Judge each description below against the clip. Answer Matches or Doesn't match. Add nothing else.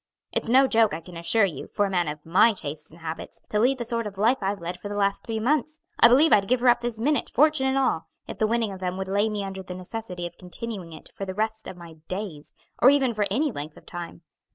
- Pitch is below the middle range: Doesn't match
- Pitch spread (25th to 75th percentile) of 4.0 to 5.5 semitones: Matches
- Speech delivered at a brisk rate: Matches